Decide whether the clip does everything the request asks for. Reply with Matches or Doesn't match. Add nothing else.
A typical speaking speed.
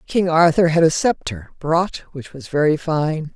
Matches